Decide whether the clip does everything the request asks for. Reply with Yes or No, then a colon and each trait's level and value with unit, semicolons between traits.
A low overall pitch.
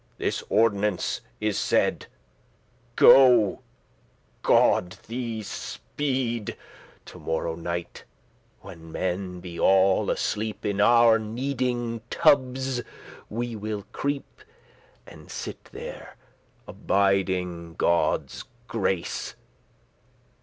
Yes: low, 105 Hz